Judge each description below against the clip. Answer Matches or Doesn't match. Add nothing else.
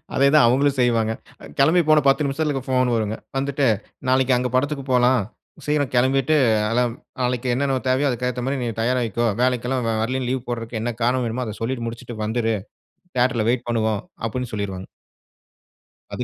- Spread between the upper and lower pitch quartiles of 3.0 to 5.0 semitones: Doesn't match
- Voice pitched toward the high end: Doesn't match